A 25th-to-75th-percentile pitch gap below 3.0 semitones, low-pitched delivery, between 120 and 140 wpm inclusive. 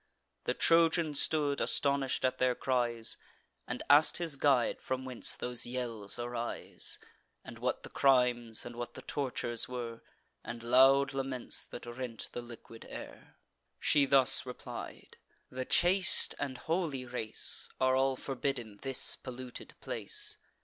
Yes: narrow, 2.4 semitones; low, 130 Hz; slow, 135 wpm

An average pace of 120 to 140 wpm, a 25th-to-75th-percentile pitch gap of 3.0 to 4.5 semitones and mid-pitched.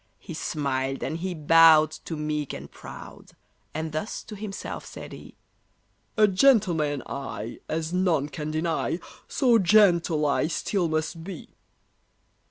Yes: slow, 135 wpm; average, 3.4 semitones; medium, 160 Hz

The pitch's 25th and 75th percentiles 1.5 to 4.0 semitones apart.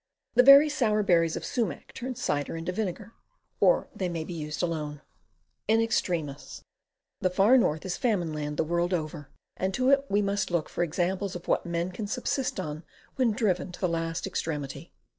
No: average, 4.9 semitones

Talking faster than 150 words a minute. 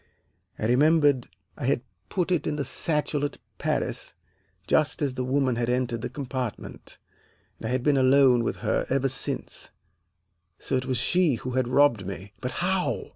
Yes: average, 175 wpm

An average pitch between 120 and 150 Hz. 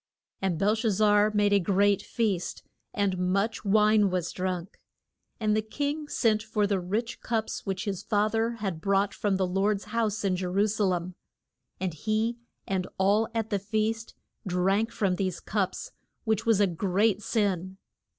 No: high, 205 Hz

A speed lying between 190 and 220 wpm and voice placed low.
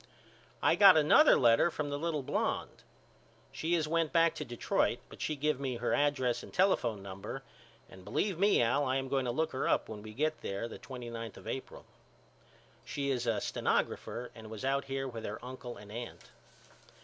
Yes: average, 195 wpm; low, 130 Hz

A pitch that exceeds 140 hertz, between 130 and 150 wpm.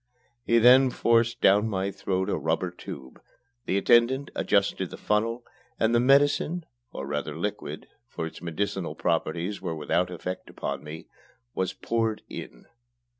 No: low, 100 Hz; average, 145 wpm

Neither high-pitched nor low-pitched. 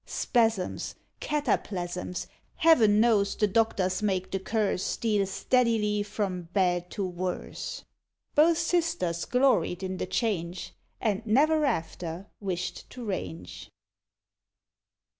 No: high, 200 Hz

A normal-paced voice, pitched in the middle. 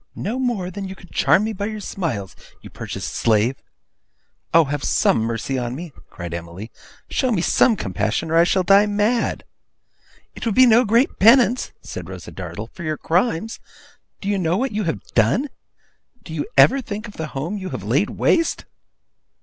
Yes: average, 185 wpm; medium, 180 Hz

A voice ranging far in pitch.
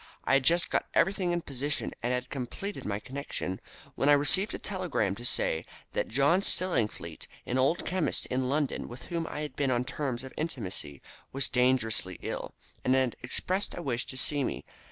No: average, 4.9 semitones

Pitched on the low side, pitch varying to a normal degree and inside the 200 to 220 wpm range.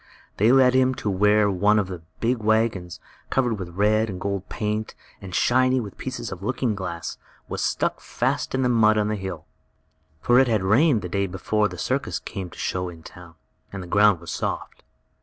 Yes: low, 105 Hz; average, 3.8 semitones; fast, 205 wpm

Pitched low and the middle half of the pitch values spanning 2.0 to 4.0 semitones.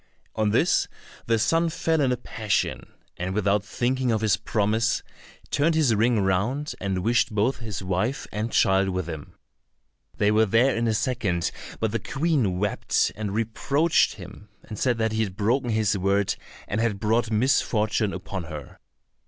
Yes: low, 110 Hz; average, 3.3 semitones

